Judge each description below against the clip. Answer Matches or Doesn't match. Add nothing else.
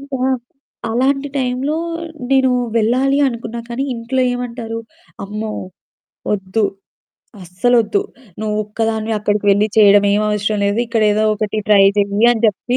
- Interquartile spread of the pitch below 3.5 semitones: Matches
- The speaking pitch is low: Doesn't match